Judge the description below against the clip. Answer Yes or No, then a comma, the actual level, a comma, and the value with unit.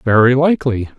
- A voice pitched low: Yes, low, 125 Hz